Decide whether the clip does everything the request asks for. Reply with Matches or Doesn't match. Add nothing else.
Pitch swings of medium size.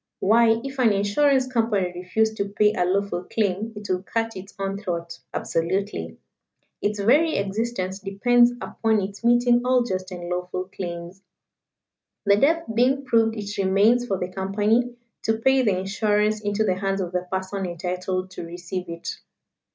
Matches